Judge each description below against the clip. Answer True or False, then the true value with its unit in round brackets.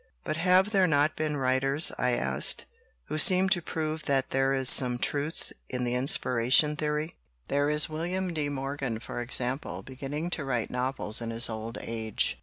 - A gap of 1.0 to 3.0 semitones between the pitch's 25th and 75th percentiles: False (3.7 semitones)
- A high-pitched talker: False (140 Hz)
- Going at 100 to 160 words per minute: False (175 wpm)